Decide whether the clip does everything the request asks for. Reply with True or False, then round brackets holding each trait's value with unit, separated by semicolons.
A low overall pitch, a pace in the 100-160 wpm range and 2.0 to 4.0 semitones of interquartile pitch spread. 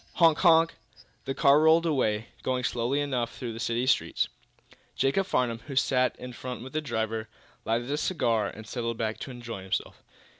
False (125 Hz; 180 wpm; 3.7 semitones)